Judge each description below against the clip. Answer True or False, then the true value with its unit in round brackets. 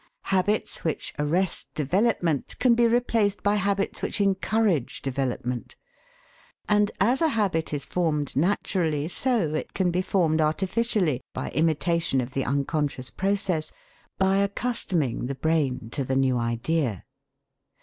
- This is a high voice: False (165 Hz)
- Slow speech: True (130 wpm)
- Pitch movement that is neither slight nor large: False (6.1 semitones)